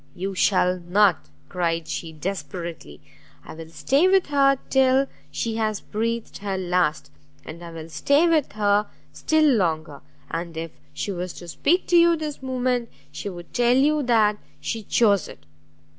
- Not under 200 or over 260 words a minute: No, average, 160 wpm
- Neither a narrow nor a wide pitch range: No, wide, 7.3 semitones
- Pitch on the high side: Yes, high, 205 Hz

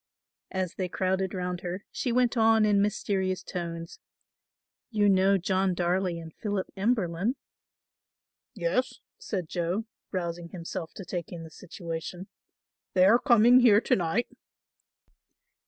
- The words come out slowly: Yes, slow, 130 wpm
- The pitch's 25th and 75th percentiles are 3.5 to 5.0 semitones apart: No, average, 3.1 semitones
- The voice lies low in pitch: No, medium, 185 Hz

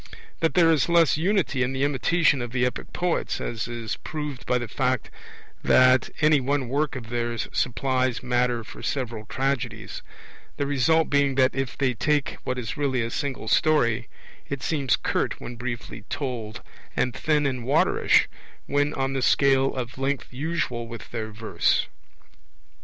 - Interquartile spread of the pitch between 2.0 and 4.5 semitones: Yes, average, 3.0 semitones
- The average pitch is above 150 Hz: No, low, 130 Hz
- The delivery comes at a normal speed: Yes, average, 165 wpm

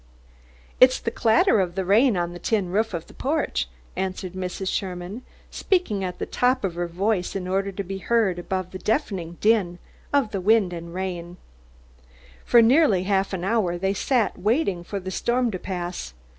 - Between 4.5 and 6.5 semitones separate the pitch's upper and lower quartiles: No, average, 3.8 semitones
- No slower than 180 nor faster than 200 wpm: Yes, average, 185 wpm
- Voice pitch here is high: Yes, high, 195 Hz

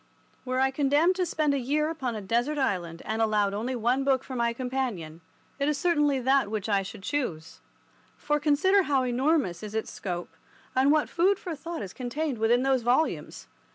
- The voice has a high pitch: Yes, very high, 260 Hz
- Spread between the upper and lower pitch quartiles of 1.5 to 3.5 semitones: No, average, 5.1 semitones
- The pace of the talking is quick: No, average, 190 wpm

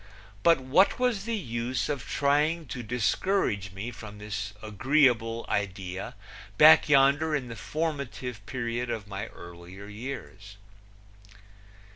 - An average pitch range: No, wide, 5.7 semitones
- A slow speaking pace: Yes, slow, 120 wpm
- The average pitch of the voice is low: Yes, low, 120 Hz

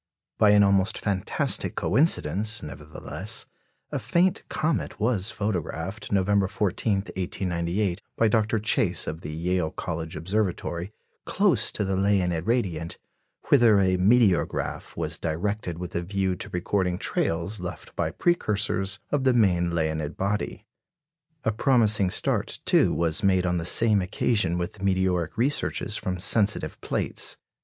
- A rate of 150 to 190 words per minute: No, slow, 135 wpm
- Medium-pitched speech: No, very low, 95 Hz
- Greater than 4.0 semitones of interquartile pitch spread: No, average, 3.4 semitones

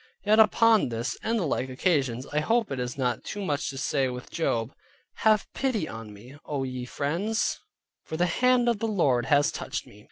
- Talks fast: Yes, fast, 210 wpm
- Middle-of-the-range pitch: Yes, medium, 145 Hz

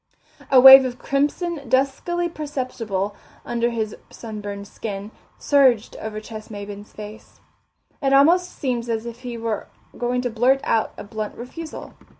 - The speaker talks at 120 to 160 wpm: Yes, average, 145 wpm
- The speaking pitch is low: No, high, 240 Hz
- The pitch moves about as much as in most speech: Yes, average, 4.0 semitones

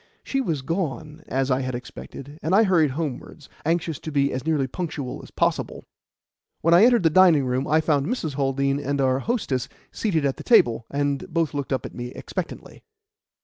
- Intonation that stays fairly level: No, average, 3.7 semitones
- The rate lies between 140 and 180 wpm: No, average, 190 wpm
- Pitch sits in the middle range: Yes, medium, 145 Hz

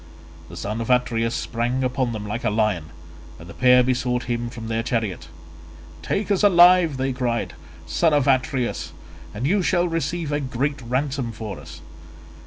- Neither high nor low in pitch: No, low, 125 Hz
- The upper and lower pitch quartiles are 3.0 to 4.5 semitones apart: Yes, average, 3.9 semitones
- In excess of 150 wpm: Yes, average, 170 wpm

